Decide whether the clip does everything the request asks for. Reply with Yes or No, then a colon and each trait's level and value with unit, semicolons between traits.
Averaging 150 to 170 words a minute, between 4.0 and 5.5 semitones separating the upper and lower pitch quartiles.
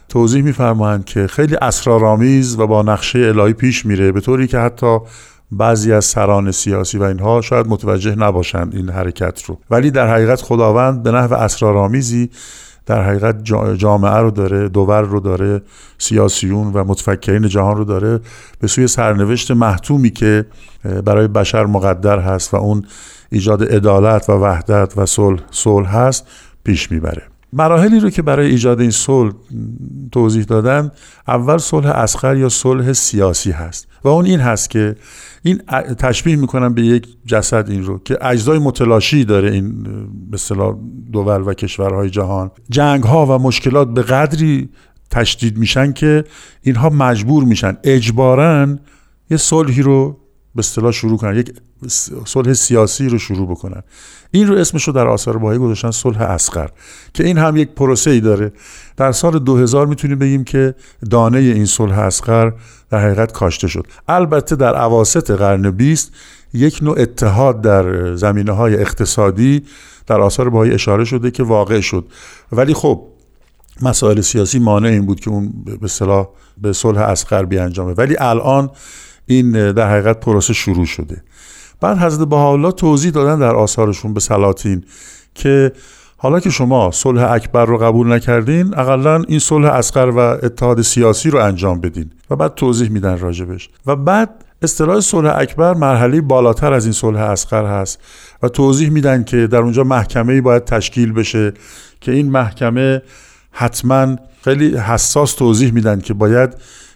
Yes: fast, 155 wpm; average, 4.3 semitones